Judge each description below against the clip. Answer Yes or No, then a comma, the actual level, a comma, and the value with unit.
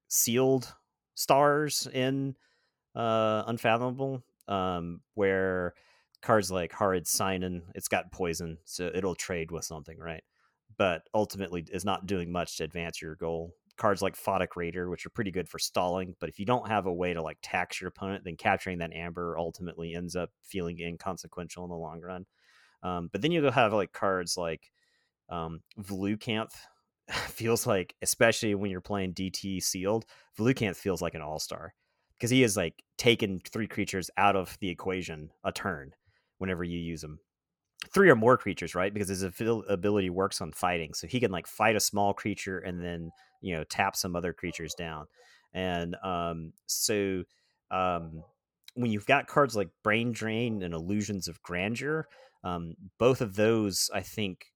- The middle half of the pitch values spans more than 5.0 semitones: No, average, 3.7 semitones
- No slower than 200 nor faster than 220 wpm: No, average, 170 wpm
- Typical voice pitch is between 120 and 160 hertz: No, very low, 95 Hz